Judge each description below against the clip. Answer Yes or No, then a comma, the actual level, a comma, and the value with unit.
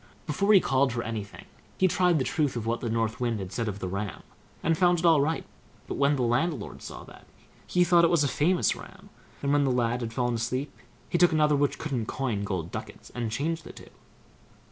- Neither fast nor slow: No, fast, 230 wpm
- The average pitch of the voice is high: No, low, 135 Hz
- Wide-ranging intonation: Yes, wide, 5.8 semitones